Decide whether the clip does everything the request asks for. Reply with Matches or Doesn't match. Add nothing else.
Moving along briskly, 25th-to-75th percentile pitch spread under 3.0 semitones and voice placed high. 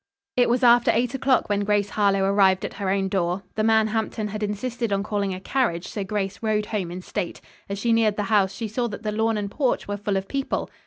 Matches